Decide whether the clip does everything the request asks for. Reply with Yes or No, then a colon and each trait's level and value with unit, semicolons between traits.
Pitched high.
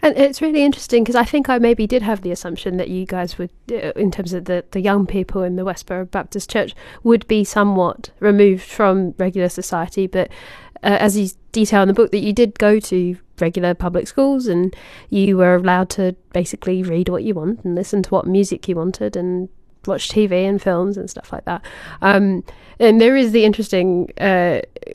Yes: high, 195 Hz